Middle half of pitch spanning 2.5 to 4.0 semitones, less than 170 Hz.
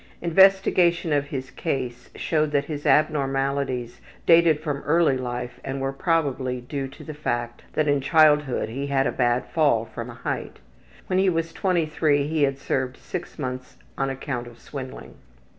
Yes: average, 3.4 semitones; medium, 140 Hz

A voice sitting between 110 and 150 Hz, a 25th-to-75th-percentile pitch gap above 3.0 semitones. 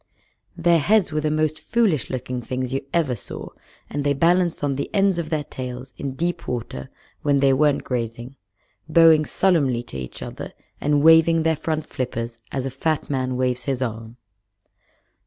Yes: medium, 140 Hz; average, 4.2 semitones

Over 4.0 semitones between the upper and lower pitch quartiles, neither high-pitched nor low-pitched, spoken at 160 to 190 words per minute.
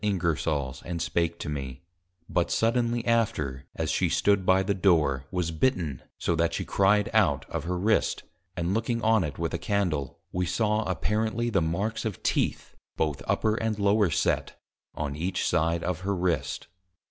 No: average, 4.6 semitones; very low, 90 Hz; average, 170 wpm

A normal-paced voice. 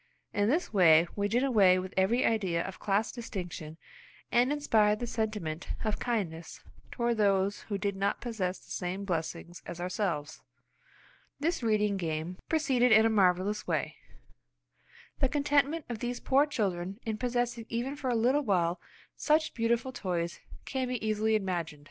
Yes: average, 155 wpm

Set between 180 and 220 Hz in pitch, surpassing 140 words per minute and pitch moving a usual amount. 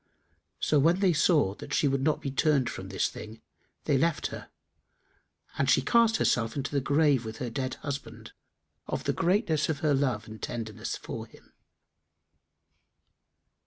No: medium, 140 Hz; average, 160 wpm; average, 4.7 semitones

